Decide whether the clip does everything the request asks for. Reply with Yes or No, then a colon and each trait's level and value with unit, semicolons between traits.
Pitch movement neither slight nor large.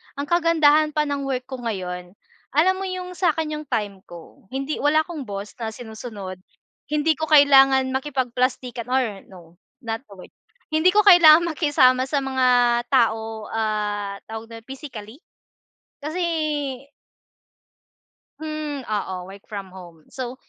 No: wide, 5.8 semitones